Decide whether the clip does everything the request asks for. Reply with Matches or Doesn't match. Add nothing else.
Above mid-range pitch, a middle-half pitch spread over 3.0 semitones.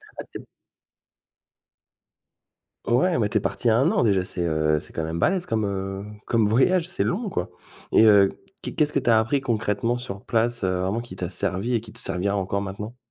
Doesn't match